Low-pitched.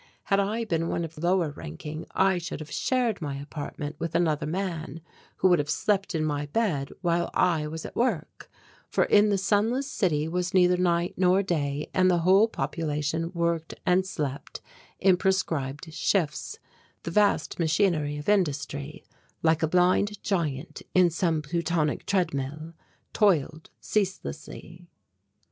No: medium, 170 Hz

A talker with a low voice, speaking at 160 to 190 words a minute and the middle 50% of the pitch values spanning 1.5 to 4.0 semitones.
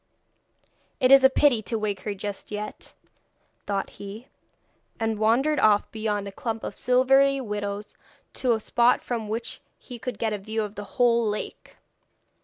No: high, 220 Hz; average, 165 wpm; average, 2.9 semitones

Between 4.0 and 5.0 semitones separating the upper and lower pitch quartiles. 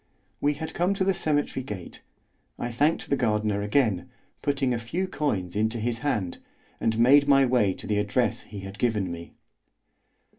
No: wide, 5.6 semitones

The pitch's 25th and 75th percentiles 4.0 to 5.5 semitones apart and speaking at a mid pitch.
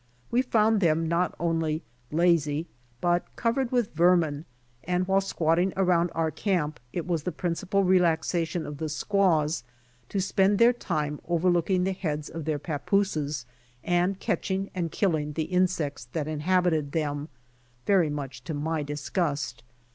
No: average, 3.4 semitones; medium, 170 Hz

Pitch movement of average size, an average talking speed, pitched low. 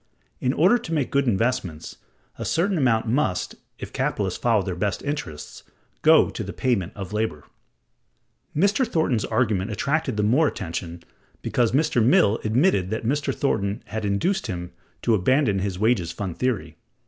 No: wide, 6.4 semitones; average, 160 wpm; low, 110 Hz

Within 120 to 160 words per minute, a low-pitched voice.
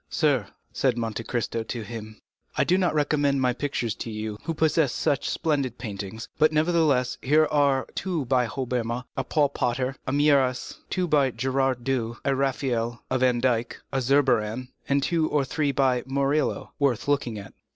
No: average, 170 wpm; low, 130 Hz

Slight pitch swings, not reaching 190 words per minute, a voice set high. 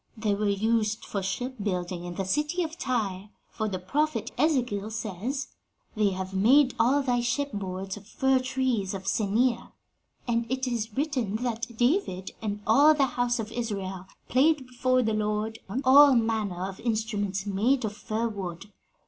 No: average, 4.2 semitones; average, 160 wpm; high, 225 Hz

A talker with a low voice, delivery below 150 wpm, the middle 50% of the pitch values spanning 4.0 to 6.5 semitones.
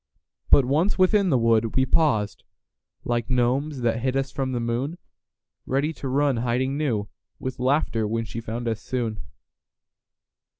No: low, 125 Hz; average, 140 wpm; average, 3.3 semitones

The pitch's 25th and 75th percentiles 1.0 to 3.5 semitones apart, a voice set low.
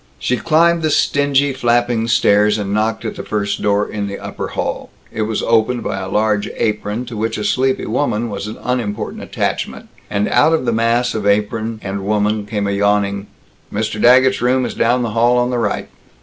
Yes: average, 2.9 semitones; low, 110 Hz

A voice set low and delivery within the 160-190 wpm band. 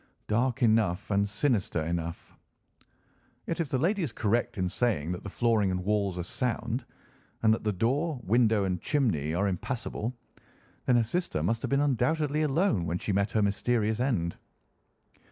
Yes: low, 110 Hz; average, 170 wpm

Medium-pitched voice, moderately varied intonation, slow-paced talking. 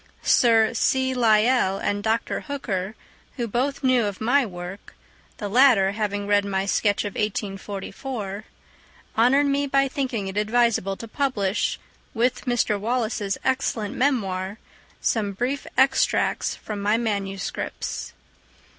No: high, 220 Hz; average, 4.0 semitones; slow, 120 wpm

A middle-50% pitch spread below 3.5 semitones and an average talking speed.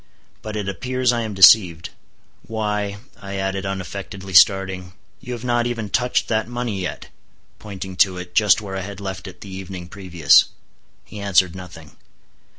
Yes: narrow, 2.5 semitones; average, 160 wpm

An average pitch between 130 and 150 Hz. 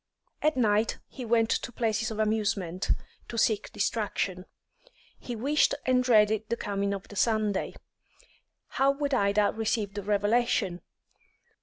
No: high, 215 Hz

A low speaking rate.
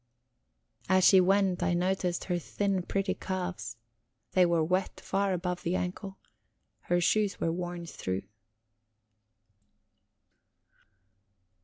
Yes: slow, 110 wpm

